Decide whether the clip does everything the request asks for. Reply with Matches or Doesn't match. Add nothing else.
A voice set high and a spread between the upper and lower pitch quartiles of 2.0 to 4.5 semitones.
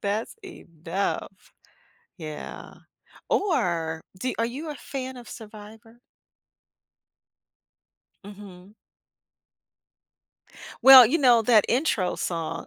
Doesn't match